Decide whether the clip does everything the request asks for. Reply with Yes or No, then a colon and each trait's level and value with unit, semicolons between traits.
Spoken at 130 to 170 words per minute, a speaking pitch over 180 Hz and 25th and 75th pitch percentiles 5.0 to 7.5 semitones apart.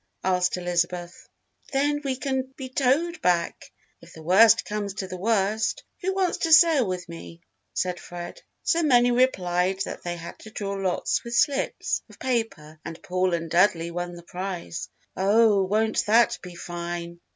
Yes: average, 165 wpm; high, 190 Hz; wide, 5.6 semitones